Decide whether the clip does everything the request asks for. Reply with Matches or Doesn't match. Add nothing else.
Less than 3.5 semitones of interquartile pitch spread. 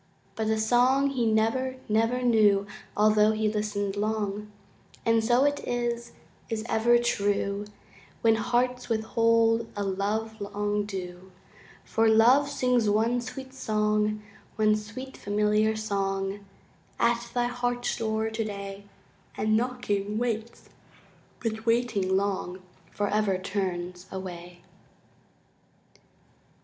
Matches